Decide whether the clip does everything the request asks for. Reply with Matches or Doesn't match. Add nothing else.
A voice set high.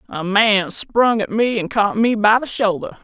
Matches